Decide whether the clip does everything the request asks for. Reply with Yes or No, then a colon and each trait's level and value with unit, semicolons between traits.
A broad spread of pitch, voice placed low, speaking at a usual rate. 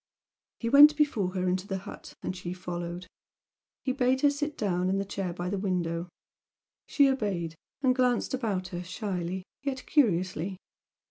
No: wide, 6.1 semitones; high, 195 Hz; average, 160 wpm